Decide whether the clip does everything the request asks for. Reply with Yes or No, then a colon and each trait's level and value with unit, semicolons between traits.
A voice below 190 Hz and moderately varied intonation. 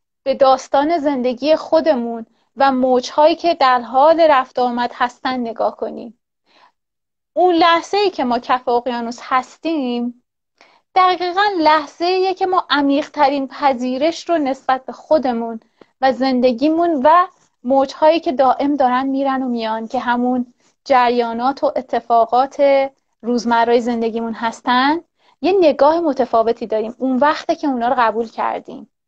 No: very high, 265 Hz; average, 4.0 semitones